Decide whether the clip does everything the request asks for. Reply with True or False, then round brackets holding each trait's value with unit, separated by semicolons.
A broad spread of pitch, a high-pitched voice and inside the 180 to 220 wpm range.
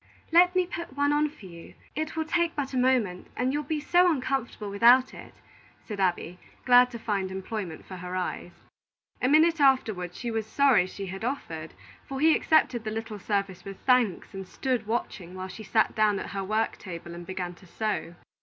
True (6.3 semitones; 220 Hz; 200 wpm)